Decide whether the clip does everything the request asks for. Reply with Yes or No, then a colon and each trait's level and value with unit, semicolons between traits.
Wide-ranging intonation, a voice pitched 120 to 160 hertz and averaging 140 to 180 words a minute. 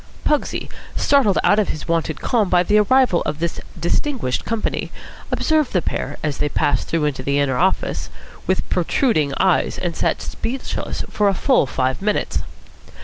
No: wide, 7.2 semitones; medium, 180 Hz; average, 165 wpm